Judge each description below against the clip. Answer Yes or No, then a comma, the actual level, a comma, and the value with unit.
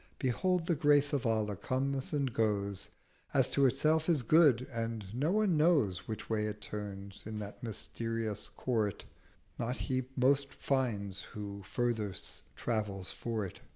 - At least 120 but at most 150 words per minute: Yes, average, 145 wpm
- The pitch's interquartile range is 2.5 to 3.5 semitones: No, average, 4.8 semitones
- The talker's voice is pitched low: Yes, low, 115 Hz